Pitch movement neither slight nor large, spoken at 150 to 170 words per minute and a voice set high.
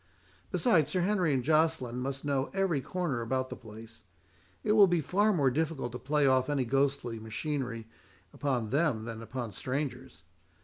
No: average, 4.4 semitones; average, 165 wpm; low, 135 Hz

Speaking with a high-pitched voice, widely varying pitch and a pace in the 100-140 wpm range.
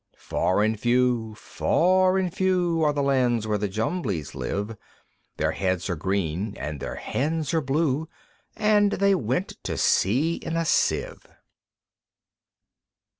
No: low, 130 Hz; wide, 8.2 semitones; slow, 135 wpm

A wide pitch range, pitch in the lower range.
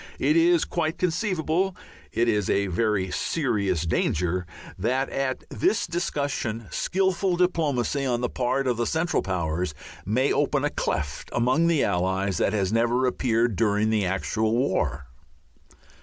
Yes: wide, 8.1 semitones; low, 120 Hz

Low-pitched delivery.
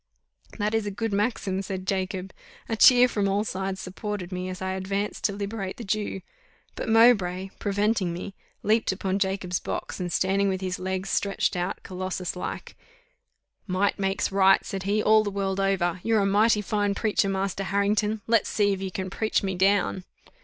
No: high, 195 Hz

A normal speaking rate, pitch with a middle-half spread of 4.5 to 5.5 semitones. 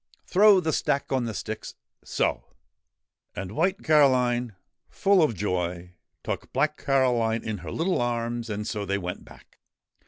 Yes: average, 160 wpm; average, 5.2 semitones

